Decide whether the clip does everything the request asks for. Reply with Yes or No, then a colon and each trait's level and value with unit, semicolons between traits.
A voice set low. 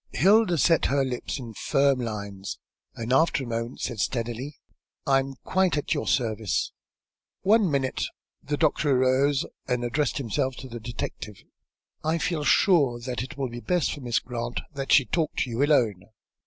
Yes: low, 130 Hz